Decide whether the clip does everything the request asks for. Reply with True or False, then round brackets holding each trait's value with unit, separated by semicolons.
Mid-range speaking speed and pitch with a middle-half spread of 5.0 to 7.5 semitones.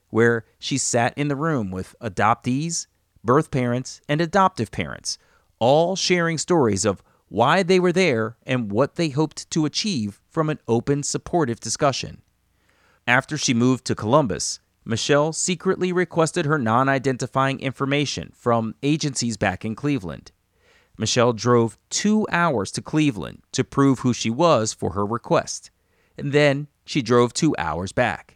True (150 wpm; 5.4 semitones)